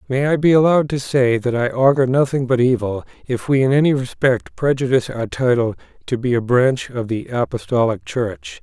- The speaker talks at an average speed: Yes, average, 195 wpm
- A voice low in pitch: Yes, low, 125 Hz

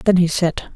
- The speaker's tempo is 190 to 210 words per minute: No, fast, 240 wpm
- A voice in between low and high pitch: Yes, medium, 175 Hz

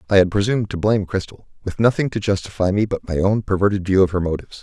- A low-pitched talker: Yes, very low, 95 Hz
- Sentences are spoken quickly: Yes, fast, 245 wpm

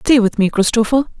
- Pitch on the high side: Yes, high, 230 Hz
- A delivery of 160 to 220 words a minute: Yes, average, 200 wpm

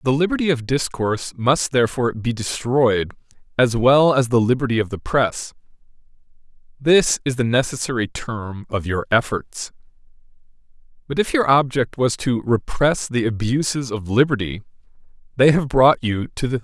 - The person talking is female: No, male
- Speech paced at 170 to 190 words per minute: No, average, 160 wpm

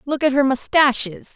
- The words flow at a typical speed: Yes, average, 175 wpm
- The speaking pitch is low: No, very high, 270 Hz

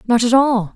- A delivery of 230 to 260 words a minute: Yes, fast, 240 wpm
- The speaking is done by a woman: Yes, female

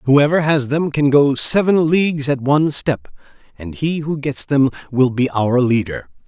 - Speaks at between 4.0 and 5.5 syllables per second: Yes, 4.5 syllables/s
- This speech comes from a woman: No, male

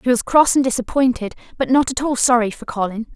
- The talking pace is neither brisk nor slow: No, fast, 230 wpm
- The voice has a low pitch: No, high, 245 Hz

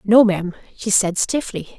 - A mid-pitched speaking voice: No, high, 200 Hz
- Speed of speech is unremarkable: Yes, average, 170 wpm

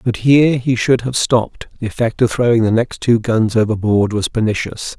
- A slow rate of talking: No, fast, 205 wpm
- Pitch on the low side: Yes, low, 115 Hz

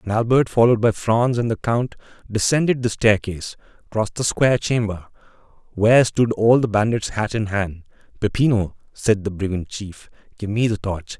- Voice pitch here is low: Yes, low, 110 Hz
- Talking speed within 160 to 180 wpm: Yes, average, 170 wpm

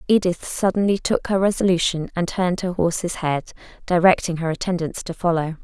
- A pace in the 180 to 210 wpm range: No, average, 160 wpm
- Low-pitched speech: No, medium, 175 Hz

